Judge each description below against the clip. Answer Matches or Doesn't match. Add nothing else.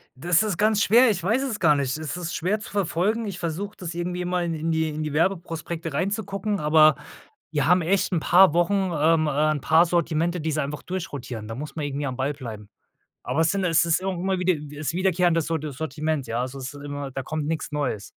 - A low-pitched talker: Doesn't match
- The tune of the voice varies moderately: Matches